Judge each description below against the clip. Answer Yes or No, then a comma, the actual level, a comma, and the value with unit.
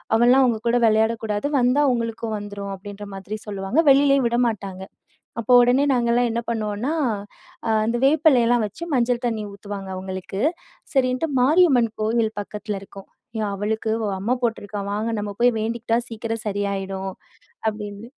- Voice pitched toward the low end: No, high, 225 Hz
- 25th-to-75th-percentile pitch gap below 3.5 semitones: Yes, average, 3.0 semitones